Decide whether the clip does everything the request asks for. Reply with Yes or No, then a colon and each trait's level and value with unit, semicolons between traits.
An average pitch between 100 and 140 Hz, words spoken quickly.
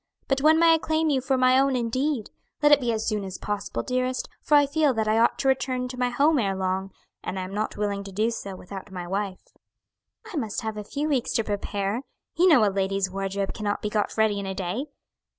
No: high, 220 Hz; fast, 240 wpm